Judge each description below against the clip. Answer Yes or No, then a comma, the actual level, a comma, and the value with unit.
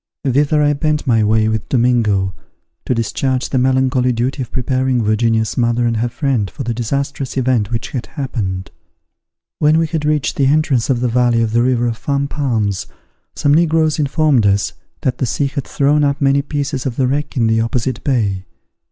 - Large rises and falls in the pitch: No, average, 3.5 semitones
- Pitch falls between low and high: No, low, 130 Hz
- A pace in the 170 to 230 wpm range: Yes, average, 190 wpm